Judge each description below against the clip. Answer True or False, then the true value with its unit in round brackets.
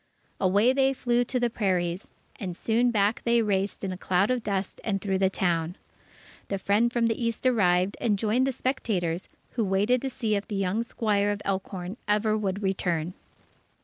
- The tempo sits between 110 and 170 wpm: False (185 wpm)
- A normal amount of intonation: True (3.6 semitones)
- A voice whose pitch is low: False (205 Hz)